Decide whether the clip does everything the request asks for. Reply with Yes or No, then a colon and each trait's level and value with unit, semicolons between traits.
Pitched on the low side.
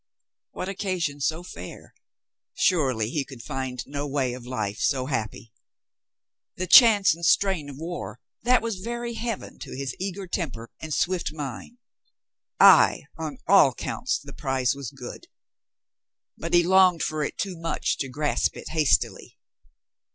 No: medium, 155 Hz